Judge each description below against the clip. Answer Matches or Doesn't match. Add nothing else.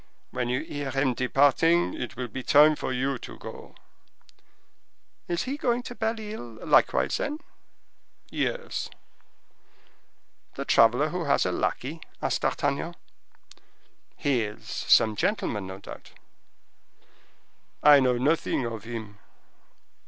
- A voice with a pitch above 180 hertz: Doesn't match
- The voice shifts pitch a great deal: Matches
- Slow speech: Matches